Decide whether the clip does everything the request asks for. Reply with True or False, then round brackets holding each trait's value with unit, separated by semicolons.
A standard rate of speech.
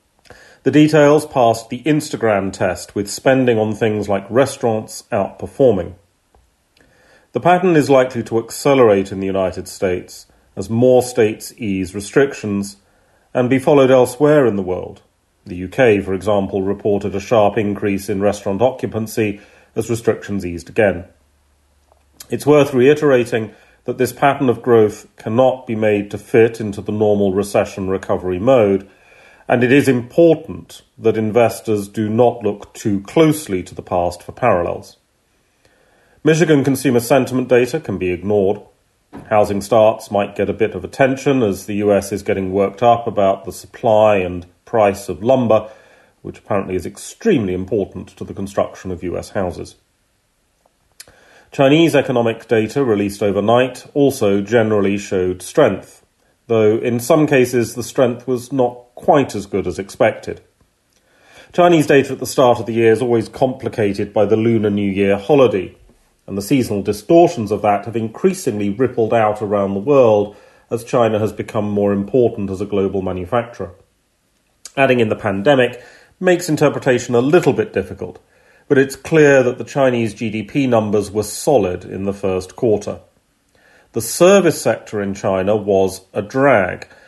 True (150 wpm)